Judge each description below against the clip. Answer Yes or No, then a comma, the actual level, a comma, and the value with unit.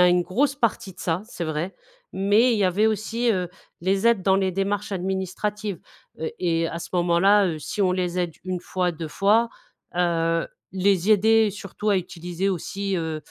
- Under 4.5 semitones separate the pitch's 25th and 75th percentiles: Yes, average, 2.8 semitones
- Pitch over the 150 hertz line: Yes, high, 190 Hz